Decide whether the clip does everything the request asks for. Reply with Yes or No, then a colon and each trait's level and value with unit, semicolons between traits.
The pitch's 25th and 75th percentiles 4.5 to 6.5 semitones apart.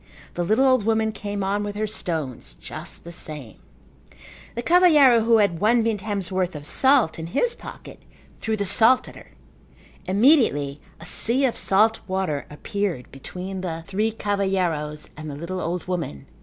Yes: average, 5.1 semitones